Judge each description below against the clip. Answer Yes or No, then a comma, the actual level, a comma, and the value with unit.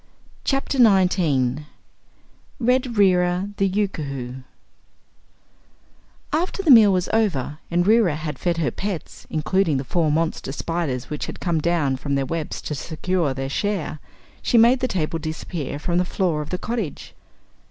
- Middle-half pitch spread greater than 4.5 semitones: Yes, average, 5.1 semitones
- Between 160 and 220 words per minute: No, average, 150 wpm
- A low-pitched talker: No, medium, 170 Hz